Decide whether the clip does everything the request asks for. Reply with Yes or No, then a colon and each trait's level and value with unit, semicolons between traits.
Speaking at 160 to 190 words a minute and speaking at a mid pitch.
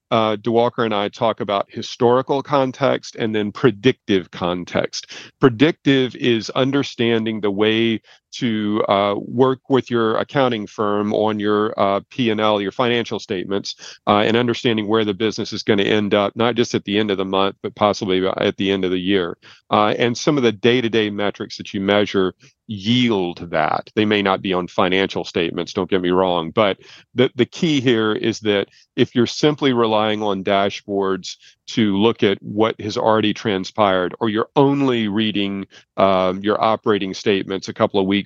No: average, 175 wpm; low, 110 Hz